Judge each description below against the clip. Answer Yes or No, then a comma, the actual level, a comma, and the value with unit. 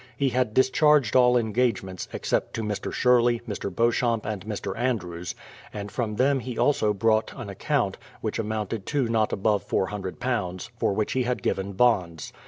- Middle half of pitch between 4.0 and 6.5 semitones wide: No, average, 3.5 semitones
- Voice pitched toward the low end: Yes, low, 110 Hz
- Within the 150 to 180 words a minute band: Yes, average, 165 wpm